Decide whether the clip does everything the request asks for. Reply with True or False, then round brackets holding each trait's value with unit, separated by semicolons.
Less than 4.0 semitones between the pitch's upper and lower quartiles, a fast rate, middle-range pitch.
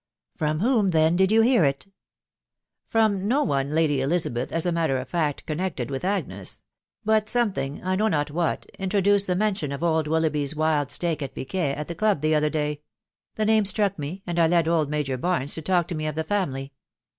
False (4.5 semitones; 225 wpm; 165 Hz)